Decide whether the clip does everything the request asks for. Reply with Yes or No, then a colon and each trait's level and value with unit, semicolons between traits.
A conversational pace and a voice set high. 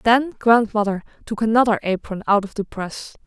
Yes: average, 165 wpm; high, 215 Hz